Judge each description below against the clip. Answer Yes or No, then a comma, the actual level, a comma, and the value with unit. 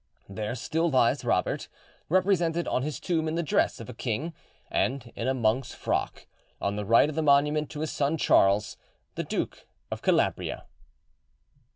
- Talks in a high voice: No, medium, 140 Hz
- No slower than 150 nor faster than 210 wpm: Yes, average, 170 wpm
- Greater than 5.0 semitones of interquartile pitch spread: Yes, wide, 5.5 semitones